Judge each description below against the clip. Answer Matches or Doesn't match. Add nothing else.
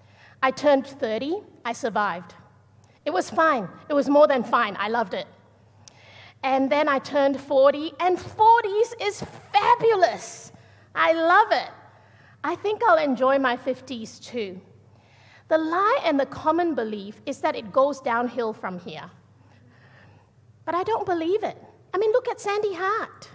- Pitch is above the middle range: Matches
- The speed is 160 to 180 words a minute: Doesn't match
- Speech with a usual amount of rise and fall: Doesn't match